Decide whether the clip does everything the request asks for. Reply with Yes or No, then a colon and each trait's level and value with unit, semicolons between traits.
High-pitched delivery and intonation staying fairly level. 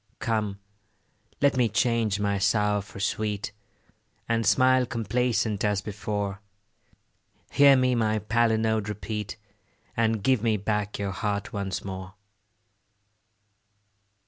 No: low, 105 Hz; narrow, 2.2 semitones